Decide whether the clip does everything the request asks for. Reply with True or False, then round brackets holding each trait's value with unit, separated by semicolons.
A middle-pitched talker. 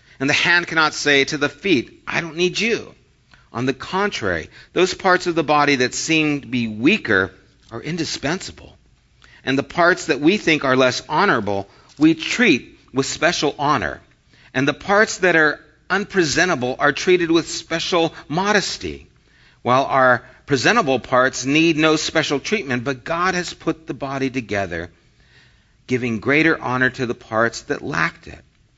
True (150 Hz)